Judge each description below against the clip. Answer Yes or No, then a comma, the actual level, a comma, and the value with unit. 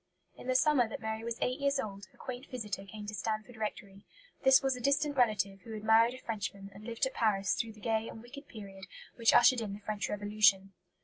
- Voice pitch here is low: No, high, 220 Hz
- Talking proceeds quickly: Yes, fast, 230 wpm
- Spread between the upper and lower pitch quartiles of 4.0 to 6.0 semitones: No, average, 3.2 semitones